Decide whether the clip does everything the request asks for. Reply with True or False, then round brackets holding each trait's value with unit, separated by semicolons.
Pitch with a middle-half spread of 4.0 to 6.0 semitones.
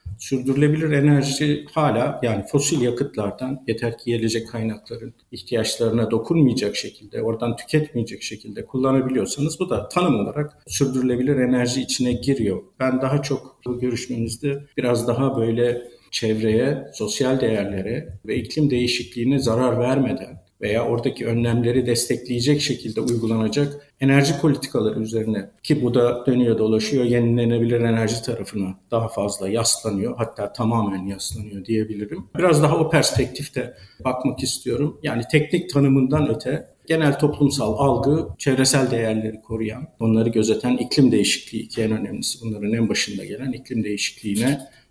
False (3.3 semitones)